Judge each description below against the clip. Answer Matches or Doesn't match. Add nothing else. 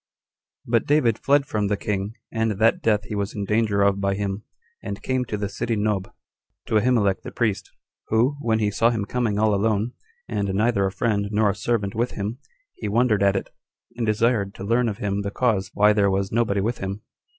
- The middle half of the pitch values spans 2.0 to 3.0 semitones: Matches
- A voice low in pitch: Matches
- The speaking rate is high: Matches